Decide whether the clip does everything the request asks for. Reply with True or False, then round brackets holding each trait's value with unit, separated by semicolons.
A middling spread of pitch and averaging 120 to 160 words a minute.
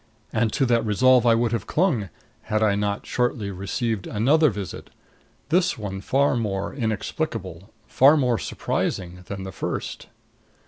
True (4.4 semitones; 145 wpm)